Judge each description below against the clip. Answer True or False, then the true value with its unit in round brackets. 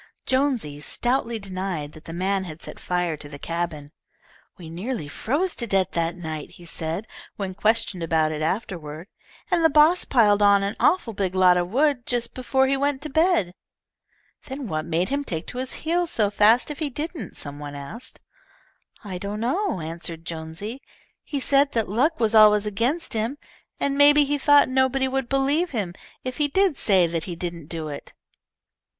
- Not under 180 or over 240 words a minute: True (185 wpm)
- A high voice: True (210 Hz)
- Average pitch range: False (8.0 semitones)